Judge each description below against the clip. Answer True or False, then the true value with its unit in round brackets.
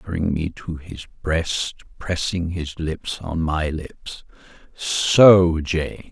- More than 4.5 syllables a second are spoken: False (3.1 syllables/s)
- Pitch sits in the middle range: False (85 Hz)